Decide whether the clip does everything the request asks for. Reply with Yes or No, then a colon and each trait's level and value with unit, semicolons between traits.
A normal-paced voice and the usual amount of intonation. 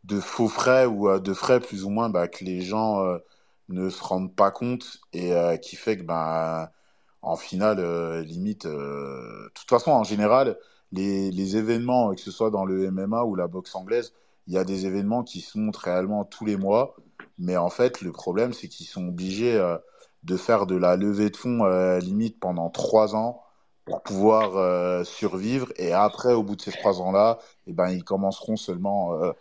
Yes: average, 210 wpm; average, 3.5 semitones